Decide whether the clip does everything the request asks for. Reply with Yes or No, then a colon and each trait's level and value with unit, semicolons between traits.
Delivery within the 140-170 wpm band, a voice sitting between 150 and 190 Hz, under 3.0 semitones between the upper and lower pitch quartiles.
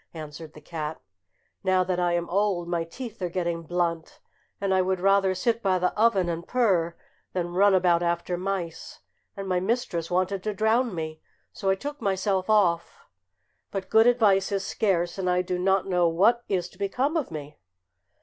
No: average, 185 wpm; medium, 185 Hz; narrow, 2.6 semitones